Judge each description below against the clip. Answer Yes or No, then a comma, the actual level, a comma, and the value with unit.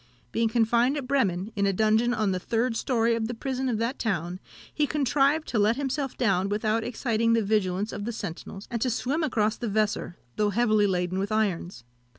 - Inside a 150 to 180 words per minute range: No, average, 200 wpm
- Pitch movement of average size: Yes, average, 3.2 semitones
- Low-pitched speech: No, high, 225 Hz